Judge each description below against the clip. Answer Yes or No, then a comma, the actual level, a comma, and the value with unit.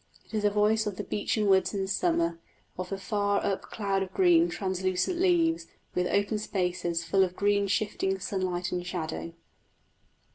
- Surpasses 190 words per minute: No, average, 170 wpm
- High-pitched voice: Yes, high, 195 Hz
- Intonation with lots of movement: No, narrow, 2.6 semitones